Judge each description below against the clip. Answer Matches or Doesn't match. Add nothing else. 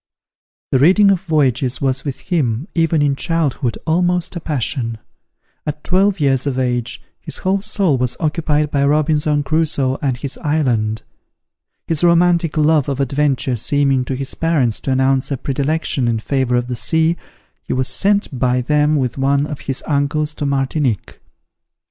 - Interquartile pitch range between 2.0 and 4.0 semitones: Matches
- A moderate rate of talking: Matches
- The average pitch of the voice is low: Doesn't match